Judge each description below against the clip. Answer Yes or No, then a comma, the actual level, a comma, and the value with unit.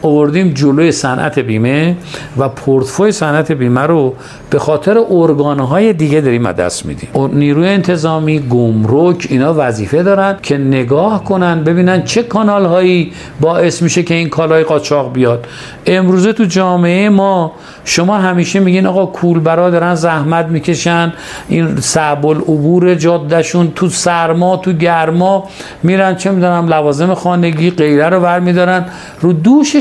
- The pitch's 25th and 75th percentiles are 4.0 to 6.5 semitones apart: No, average, 3.3 semitones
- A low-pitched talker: No, medium, 170 Hz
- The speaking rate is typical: Yes, average, 135 wpm